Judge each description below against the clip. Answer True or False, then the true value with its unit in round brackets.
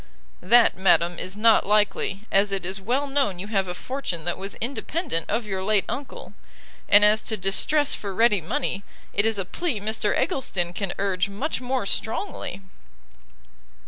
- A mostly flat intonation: False (3.9 semitones)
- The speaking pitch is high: True (205 Hz)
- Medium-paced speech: True (170 wpm)